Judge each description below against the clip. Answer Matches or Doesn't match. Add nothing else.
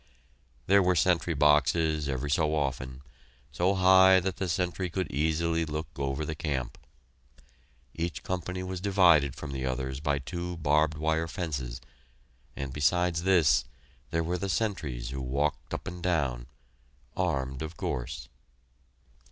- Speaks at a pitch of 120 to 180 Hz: Doesn't match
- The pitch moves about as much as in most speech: Matches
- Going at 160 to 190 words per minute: Doesn't match